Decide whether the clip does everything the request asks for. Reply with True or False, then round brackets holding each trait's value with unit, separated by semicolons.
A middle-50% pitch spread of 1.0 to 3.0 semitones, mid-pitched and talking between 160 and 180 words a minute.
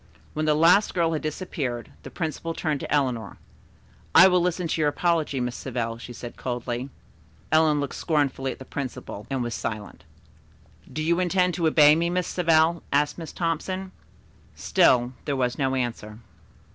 False (4.9 semitones; 150 Hz; 170 wpm)